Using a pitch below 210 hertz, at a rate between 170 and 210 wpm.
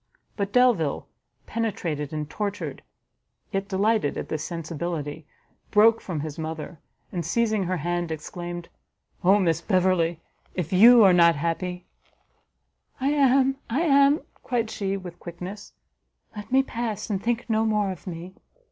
No: medium, 185 Hz; average, 145 wpm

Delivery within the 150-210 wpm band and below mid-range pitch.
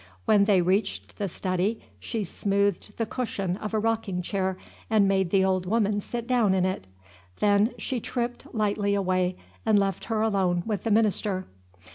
No: average, 170 wpm; high, 200 Hz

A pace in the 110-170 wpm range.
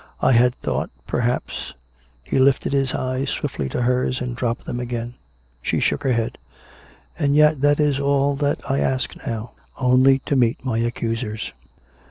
No: average, 180 wpm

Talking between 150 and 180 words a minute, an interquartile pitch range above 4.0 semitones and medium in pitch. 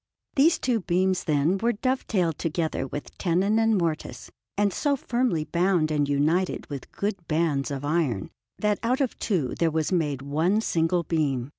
Yes: average, 170 wpm; average, 5.3 semitones; medium, 170 Hz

